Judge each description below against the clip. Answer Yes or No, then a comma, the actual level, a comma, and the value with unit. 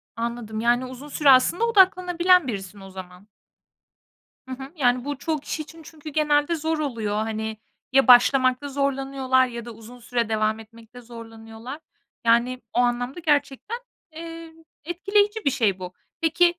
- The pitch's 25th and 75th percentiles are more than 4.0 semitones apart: Yes, average, 5.1 semitones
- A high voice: Yes, very high, 255 Hz